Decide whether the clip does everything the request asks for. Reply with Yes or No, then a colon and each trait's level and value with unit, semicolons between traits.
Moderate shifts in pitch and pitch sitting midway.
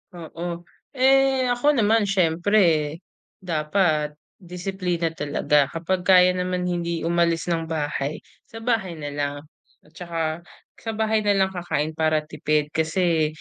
Yes: average, 3.8 semitones; medium, 175 Hz